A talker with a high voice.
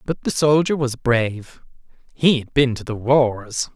No: low, 125 Hz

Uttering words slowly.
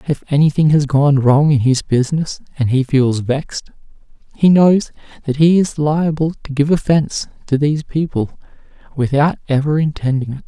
No: average, 160 wpm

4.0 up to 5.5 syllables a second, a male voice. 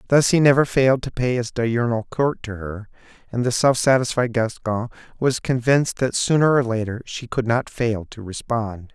Yes: 4.9 syllables/s; male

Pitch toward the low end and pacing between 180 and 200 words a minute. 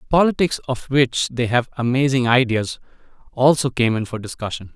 No: low, 125 Hz; average, 150 wpm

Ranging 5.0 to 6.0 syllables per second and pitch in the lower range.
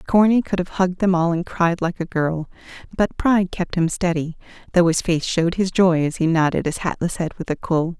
No: 5.4 syllables/s; medium, 175 Hz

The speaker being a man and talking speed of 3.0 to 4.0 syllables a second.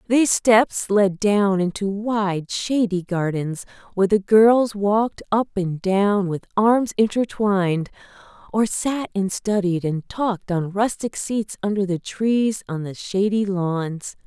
No: female; 3.8 syllables/s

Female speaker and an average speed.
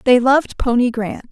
Yes: female; average, 185 wpm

